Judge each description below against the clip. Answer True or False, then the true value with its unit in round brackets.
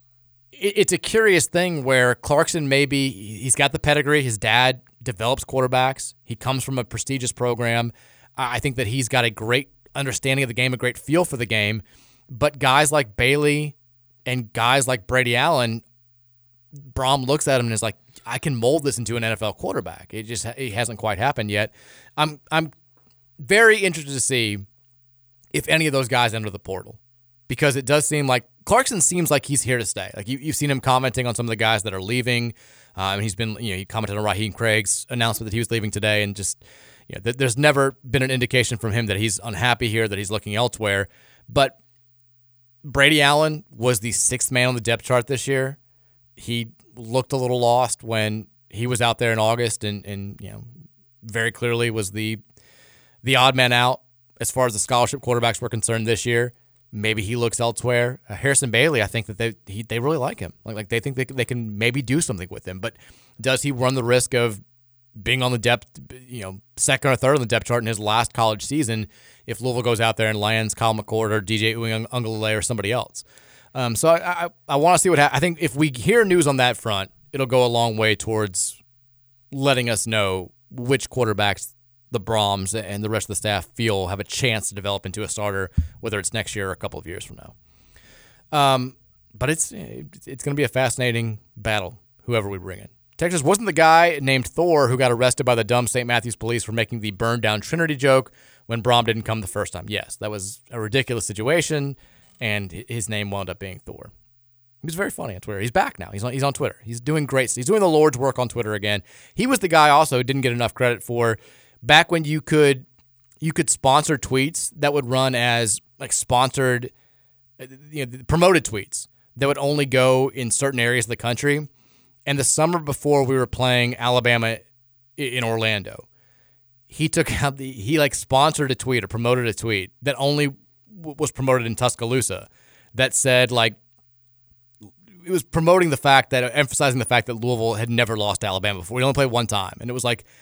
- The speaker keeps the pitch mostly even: False (3.2 semitones)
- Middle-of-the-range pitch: False (120 Hz)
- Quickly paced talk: True (210 wpm)